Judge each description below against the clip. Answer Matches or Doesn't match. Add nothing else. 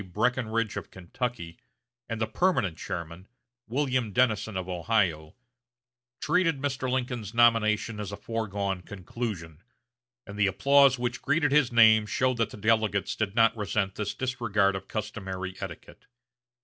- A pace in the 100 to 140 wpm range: Matches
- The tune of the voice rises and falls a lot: Doesn't match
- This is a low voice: Matches